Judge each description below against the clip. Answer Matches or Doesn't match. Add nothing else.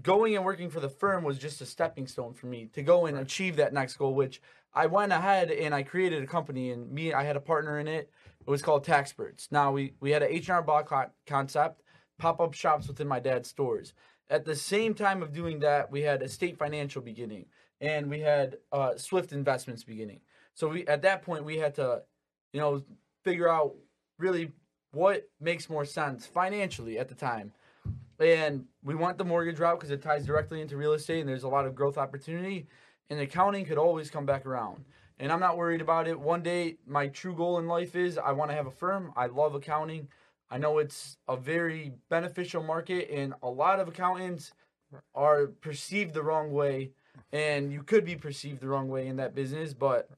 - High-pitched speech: Doesn't match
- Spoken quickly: Matches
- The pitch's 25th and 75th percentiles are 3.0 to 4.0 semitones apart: Matches